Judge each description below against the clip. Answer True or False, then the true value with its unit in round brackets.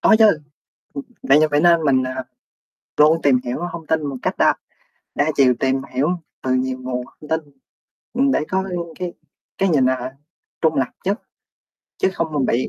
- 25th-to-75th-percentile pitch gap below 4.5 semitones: True (4.1 semitones)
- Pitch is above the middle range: False (145 Hz)